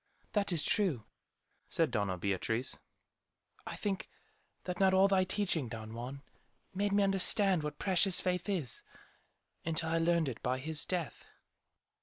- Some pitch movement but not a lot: No, wide, 6.8 semitones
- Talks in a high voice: No, medium, 165 Hz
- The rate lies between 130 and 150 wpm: Yes, average, 145 wpm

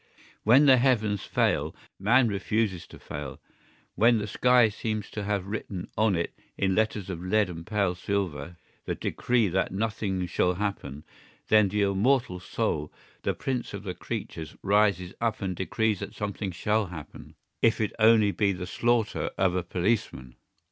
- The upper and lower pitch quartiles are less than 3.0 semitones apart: No, average, 3.3 semitones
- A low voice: Yes, low, 100 Hz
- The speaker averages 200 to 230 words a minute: No, average, 160 wpm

